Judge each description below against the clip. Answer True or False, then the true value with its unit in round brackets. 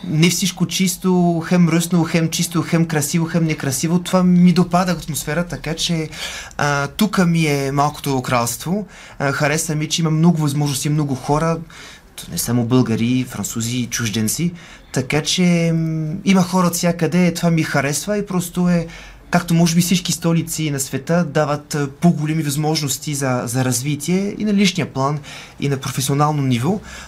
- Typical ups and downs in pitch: True (3.5 semitones)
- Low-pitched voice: False (160 Hz)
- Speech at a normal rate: True (155 wpm)